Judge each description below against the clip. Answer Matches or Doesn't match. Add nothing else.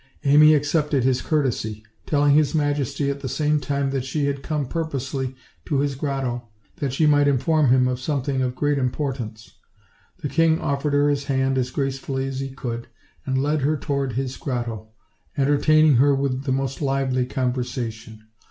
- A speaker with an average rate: Matches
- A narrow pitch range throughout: Matches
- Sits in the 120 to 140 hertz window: Matches